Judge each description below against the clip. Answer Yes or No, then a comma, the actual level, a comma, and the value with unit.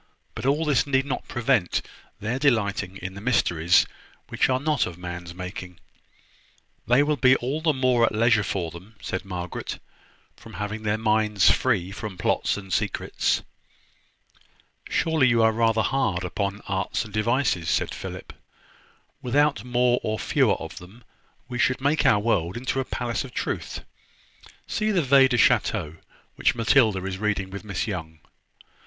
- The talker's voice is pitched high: No, low, 110 Hz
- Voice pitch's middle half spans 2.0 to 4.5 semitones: No, average, 5.2 semitones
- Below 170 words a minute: Yes, average, 160 wpm